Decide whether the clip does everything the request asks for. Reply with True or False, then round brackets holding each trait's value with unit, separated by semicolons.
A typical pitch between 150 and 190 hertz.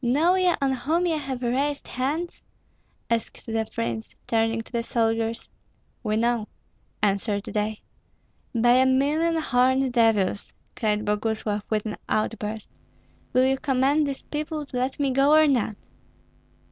False (245 Hz)